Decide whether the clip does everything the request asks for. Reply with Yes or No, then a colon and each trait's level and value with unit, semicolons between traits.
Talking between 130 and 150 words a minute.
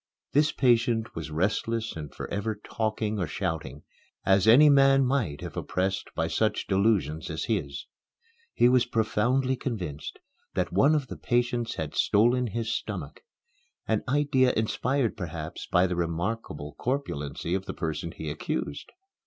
Yes: average, 145 wpm